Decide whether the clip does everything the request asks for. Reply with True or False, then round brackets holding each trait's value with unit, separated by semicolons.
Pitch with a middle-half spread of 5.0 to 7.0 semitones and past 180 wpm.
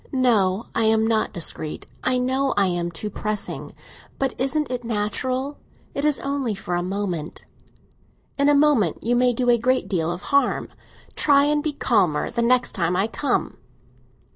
False (5.5 semitones; 170 wpm)